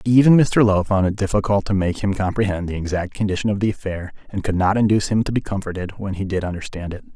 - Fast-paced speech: Yes, fast, 245 wpm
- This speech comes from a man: Yes, male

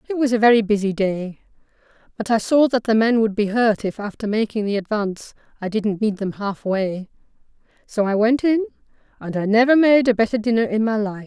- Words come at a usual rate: No, fast, 210 wpm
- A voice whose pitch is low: No, high, 220 Hz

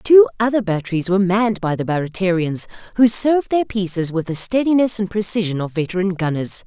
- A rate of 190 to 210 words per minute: No, average, 180 wpm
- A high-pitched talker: Yes, high, 195 Hz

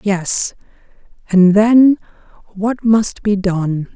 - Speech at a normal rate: No, slow, 105 wpm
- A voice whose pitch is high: Yes, high, 205 Hz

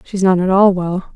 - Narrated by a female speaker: Yes, female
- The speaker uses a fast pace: Yes, fast, 260 wpm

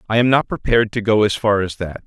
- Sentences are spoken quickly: Yes, fast, 290 wpm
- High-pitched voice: No, low, 110 Hz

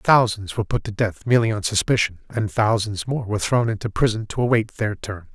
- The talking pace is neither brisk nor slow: No, fast, 215 wpm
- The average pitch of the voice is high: No, low, 110 Hz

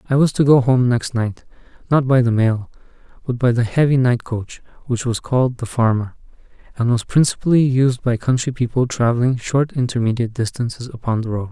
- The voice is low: Yes, low, 125 Hz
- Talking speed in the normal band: Yes, average, 190 wpm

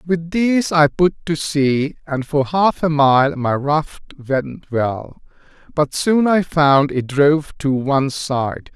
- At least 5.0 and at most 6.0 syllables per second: No, 3.6 syllables/s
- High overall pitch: No, medium, 150 Hz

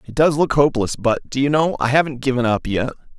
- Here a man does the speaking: Yes, male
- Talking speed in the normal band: No, fast, 245 wpm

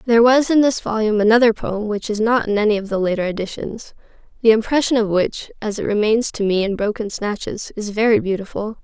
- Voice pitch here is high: Yes, high, 220 Hz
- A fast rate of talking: Yes, fast, 210 wpm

